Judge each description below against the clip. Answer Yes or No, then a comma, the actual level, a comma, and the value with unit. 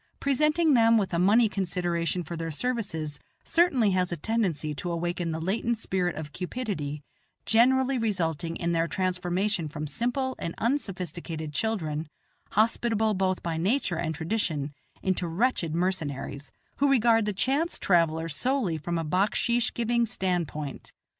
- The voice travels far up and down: Yes, wide, 5.8 semitones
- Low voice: No, medium, 185 Hz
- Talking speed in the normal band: Yes, average, 145 wpm